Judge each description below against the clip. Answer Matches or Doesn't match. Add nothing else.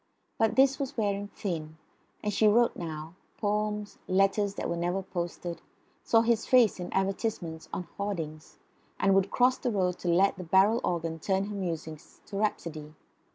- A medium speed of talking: Matches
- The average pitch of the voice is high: Matches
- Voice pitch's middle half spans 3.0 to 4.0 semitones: Matches